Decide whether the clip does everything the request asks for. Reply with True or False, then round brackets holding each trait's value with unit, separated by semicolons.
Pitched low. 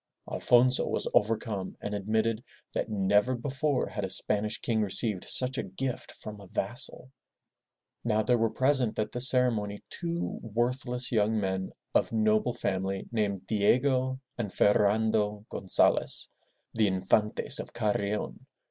True (110 Hz)